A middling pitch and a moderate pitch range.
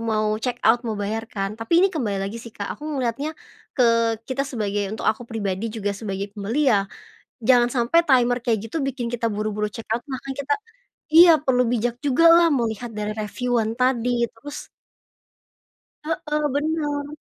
No: high, 235 Hz; average, 4.1 semitones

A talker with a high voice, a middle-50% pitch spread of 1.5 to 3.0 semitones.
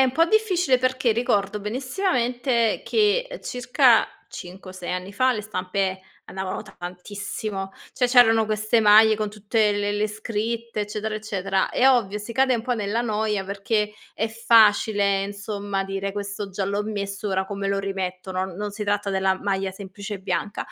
Yes: high, 210 Hz; average, 2.7 semitones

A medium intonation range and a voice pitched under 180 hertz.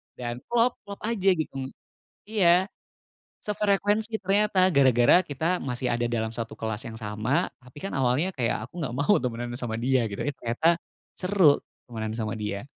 No: wide, 8.2 semitones; low, 135 Hz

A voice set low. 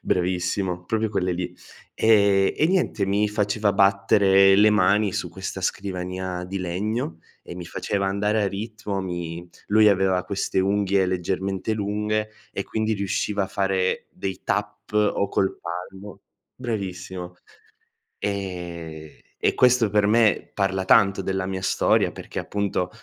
Yes: low, 100 Hz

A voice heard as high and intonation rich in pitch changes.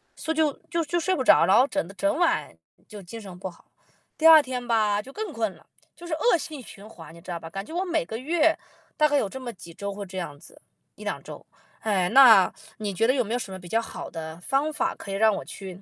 Yes: high, 230 Hz; wide, 7.8 semitones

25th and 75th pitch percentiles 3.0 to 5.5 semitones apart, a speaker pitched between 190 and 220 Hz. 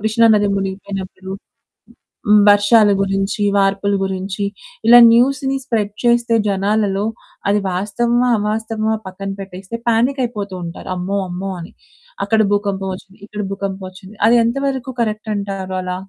No: narrow, 2.6 semitones; high, 205 Hz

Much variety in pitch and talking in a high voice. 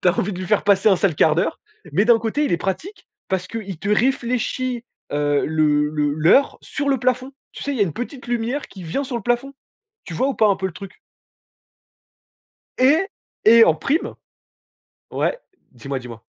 Yes: wide, 7.3 semitones; high, 210 Hz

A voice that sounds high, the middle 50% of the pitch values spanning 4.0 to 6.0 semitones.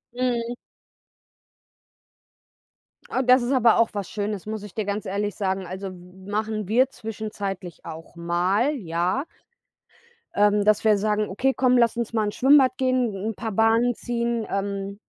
No: high, 215 Hz; average, 3.2 semitones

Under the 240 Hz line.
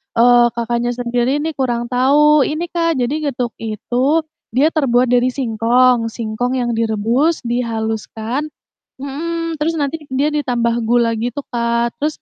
No: high, 245 Hz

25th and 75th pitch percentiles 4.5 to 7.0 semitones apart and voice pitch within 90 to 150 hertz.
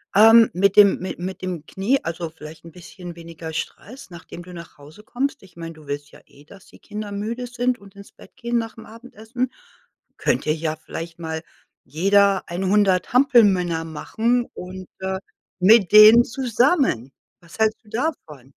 No: average, 5.2 semitones; high, 190 Hz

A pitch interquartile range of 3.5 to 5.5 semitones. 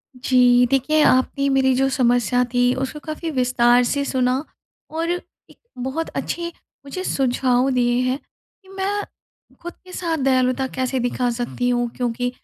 No: average, 2.8 semitones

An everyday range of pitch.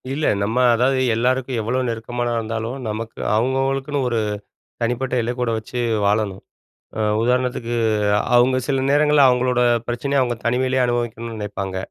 No: narrow, 2.3 semitones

